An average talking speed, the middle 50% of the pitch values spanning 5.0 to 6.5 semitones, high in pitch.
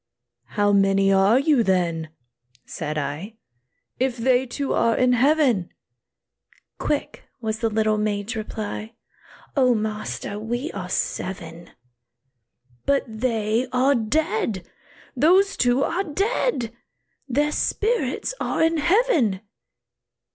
No: slow, 110 wpm; wide, 5.4 semitones; high, 230 Hz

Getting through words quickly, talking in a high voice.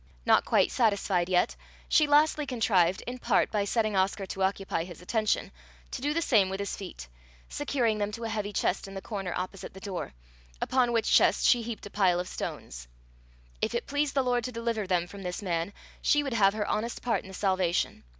Yes: fast, 210 wpm; high, 205 Hz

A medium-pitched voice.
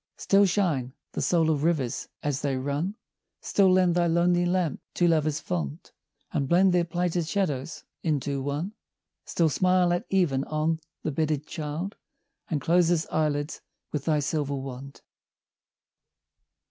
Yes: medium, 160 Hz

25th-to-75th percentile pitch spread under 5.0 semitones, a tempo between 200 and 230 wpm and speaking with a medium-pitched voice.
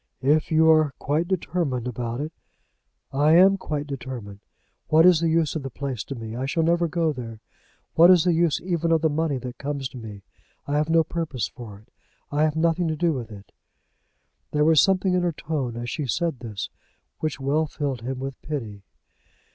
Yes: average, 4.3 semitones; fast, 205 wpm; medium, 150 Hz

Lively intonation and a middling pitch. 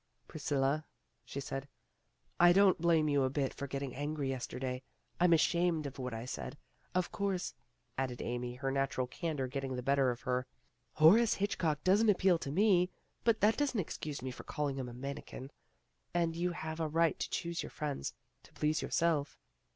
No: average, 4.5 semitones; medium, 150 Hz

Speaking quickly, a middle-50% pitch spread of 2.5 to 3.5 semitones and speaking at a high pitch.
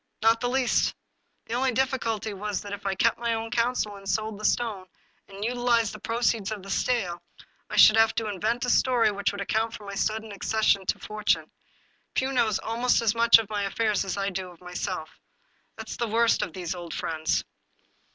Yes: fast, 210 wpm; average, 2.8 semitones; high, 215 Hz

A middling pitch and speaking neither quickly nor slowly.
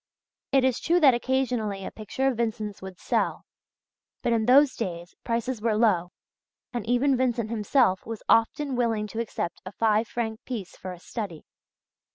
No: high, 230 Hz; average, 170 wpm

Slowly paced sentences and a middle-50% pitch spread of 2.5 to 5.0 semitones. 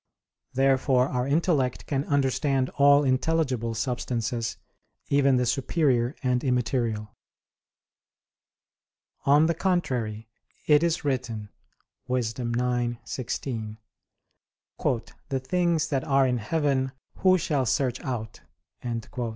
Yes: slow, 95 wpm; average, 3.0 semitones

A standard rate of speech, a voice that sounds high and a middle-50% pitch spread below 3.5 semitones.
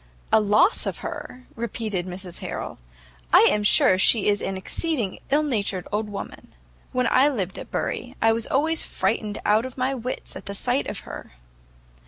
No: average, 180 wpm; high, 220 Hz; average, 4.5 semitones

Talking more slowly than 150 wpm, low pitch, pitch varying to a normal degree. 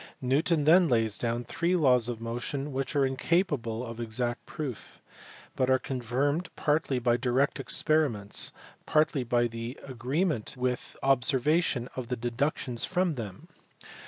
Yes: slow, 135 wpm; low, 130 Hz; average, 3.8 semitones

